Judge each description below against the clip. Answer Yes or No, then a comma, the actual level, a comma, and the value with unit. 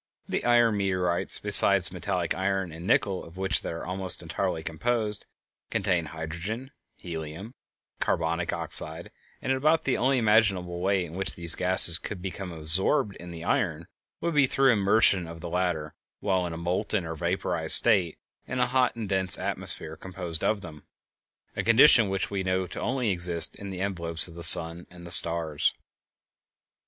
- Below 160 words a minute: No, average, 175 wpm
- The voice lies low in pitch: Yes, very low, 90 Hz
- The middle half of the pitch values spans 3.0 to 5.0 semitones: Yes, average, 3.5 semitones